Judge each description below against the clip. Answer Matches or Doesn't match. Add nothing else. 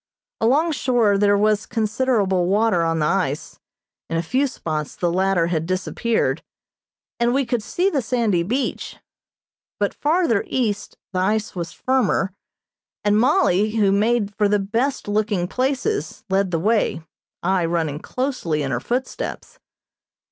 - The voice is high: Matches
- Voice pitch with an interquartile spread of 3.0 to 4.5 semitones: Doesn't match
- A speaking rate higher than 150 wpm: Doesn't match